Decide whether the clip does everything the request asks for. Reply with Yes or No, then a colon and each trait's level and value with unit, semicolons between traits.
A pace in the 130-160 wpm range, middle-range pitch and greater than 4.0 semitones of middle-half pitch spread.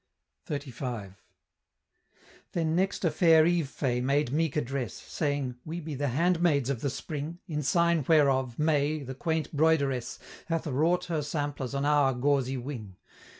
No: average, 150 wpm; medium, 145 Hz; average, 3.3 semitones